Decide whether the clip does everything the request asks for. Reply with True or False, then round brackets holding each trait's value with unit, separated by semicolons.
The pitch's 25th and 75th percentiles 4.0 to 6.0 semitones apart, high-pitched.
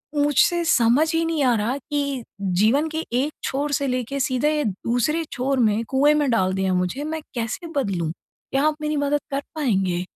True (4.8 semitones; 270 Hz)